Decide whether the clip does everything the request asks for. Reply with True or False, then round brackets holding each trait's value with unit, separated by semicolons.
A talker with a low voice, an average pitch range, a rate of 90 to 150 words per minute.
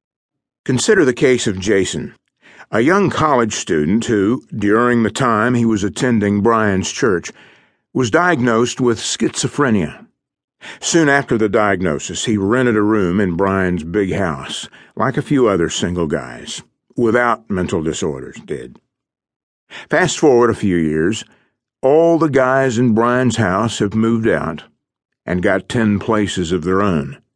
True (110 Hz; 3.4 semitones; 145 wpm)